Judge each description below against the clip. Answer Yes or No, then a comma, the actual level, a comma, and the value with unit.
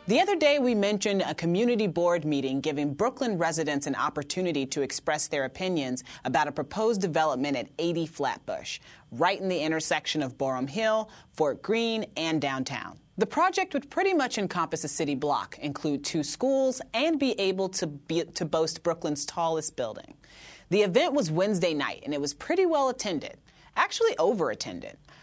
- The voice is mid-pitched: Yes, medium, 170 Hz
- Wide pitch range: Yes, wide, 6.6 semitones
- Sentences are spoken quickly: No, average, 170 wpm